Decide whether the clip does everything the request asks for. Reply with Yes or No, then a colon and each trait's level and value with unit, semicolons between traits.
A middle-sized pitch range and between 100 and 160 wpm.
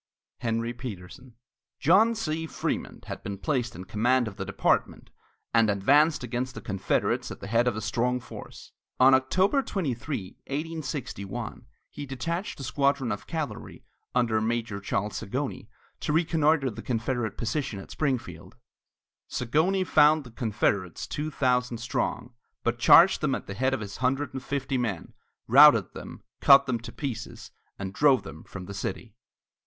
Yes: average, 4.7 semitones; average, 155 wpm